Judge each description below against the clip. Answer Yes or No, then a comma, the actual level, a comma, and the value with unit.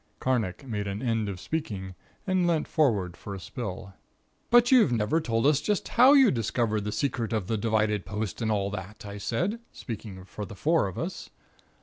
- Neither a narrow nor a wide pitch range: No, wide, 6.3 semitones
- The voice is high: No, low, 110 Hz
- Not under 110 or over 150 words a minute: No, average, 195 wpm